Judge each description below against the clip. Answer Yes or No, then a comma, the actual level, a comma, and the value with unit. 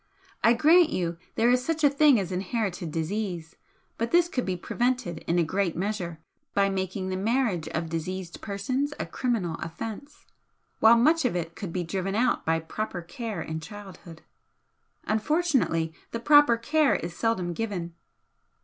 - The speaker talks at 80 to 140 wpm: No, average, 160 wpm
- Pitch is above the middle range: Yes, high, 200 Hz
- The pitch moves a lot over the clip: Yes, wide, 6.1 semitones